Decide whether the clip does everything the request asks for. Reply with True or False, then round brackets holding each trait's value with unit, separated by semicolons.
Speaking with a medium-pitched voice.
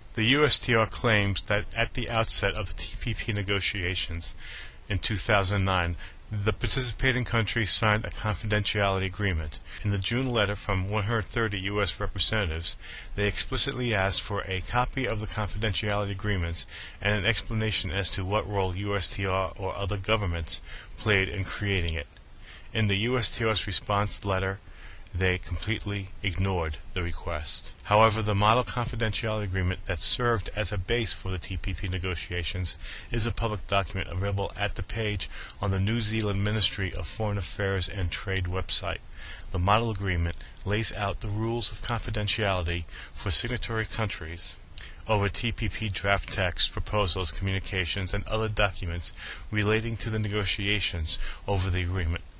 False (100 Hz)